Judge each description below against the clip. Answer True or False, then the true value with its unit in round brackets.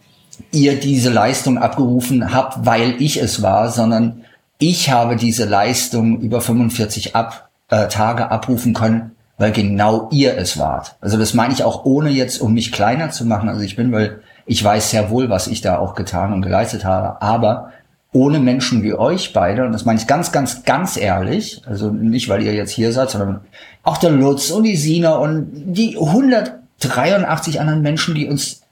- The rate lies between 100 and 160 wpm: False (185 wpm)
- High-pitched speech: False (120 Hz)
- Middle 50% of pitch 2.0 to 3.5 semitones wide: False (4.0 semitones)